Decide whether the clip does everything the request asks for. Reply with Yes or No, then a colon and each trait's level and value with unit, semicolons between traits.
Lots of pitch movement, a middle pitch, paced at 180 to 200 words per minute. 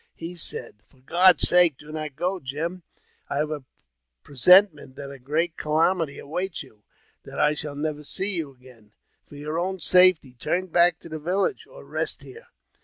No: average, 4.0 semitones; medium, 155 Hz; average, 190 wpm